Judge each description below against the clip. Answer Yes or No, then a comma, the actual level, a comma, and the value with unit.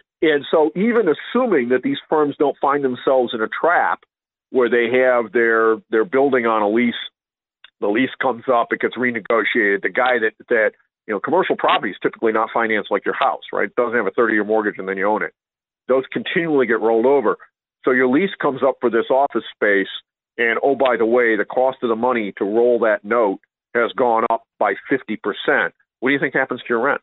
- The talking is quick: Yes, fast, 220 wpm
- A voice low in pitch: Yes, low, 125 Hz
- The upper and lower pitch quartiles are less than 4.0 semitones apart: No, average, 4.3 semitones